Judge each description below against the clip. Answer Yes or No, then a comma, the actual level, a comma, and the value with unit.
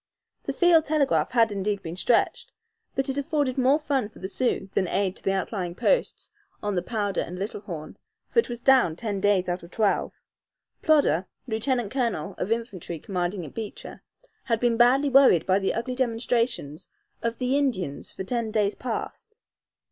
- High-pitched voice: Yes, high, 225 Hz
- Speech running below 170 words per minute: No, average, 180 wpm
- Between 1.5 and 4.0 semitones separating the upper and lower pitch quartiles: No, average, 5.3 semitones